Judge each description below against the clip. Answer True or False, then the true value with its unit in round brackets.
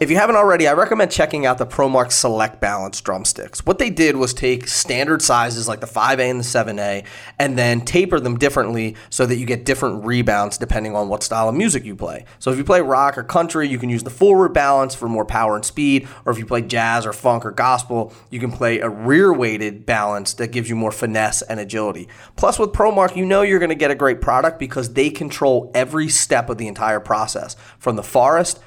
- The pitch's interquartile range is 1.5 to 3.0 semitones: False (3.7 semitones)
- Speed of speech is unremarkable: False (230 wpm)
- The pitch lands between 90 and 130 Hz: True (125 Hz)